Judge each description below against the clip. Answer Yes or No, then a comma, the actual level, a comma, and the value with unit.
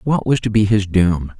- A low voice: Yes, low, 105 Hz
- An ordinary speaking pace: No, fast, 260 wpm